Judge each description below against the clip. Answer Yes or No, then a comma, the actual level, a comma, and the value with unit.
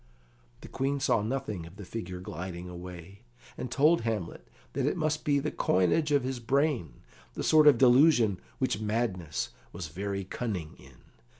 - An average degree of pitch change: No, wide, 7.1 semitones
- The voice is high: No, low, 110 Hz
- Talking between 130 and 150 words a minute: No, average, 165 wpm